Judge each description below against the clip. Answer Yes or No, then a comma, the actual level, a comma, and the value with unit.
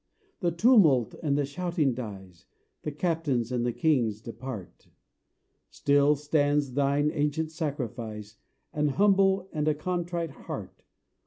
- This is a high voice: No, medium, 145 Hz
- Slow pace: Yes, slow, 120 wpm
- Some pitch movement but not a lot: Yes, average, 4.7 semitones